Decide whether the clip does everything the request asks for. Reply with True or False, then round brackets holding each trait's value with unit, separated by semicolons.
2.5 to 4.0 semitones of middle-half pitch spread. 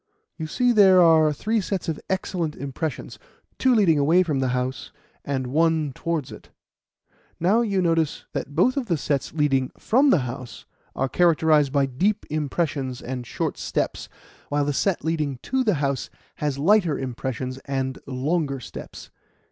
False (4.8 semitones)